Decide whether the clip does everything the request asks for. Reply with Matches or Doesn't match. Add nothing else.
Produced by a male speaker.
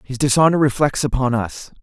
Matches